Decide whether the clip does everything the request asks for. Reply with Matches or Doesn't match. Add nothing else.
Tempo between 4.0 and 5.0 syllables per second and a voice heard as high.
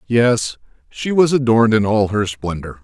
Doesn't match